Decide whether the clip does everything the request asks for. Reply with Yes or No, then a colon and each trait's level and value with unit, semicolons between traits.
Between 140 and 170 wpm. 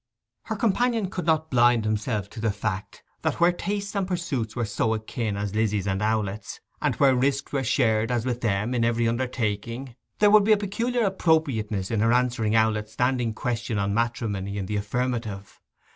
No: average, 185 wpm